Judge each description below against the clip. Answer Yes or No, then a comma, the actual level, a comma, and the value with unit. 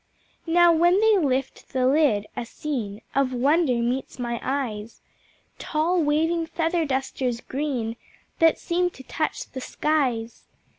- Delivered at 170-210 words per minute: No, slow, 135 wpm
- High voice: Yes, very high, 275 Hz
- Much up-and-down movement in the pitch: No, average, 4.8 semitones